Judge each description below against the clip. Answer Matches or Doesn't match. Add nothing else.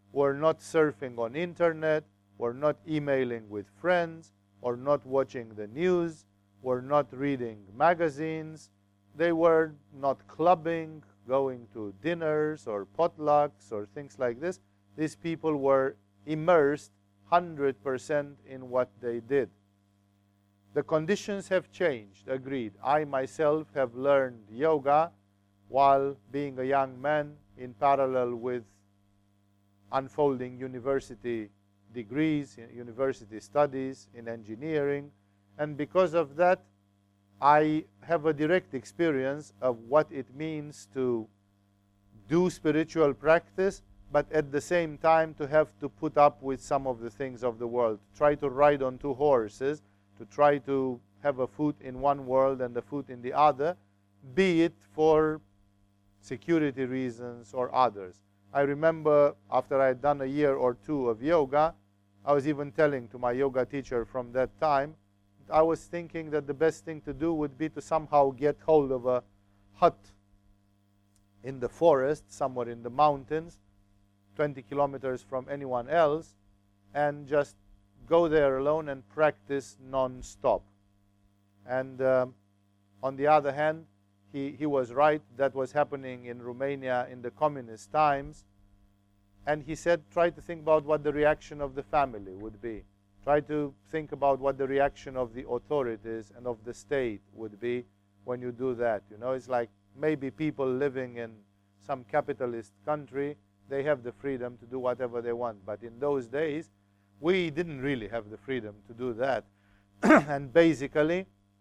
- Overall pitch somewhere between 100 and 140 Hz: Matches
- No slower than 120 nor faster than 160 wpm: Matches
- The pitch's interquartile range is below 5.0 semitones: Doesn't match